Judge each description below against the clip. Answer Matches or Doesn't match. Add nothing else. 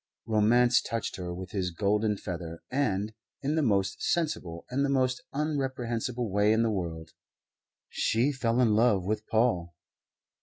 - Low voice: Matches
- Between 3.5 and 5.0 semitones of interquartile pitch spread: Matches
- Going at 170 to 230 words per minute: Doesn't match